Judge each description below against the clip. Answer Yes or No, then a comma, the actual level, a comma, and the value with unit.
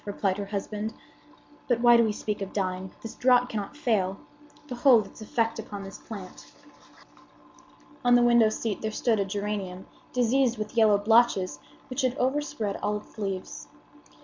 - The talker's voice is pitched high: Yes, high, 215 Hz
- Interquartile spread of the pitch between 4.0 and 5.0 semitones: No, average, 3.2 semitones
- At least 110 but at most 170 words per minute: Yes, average, 160 wpm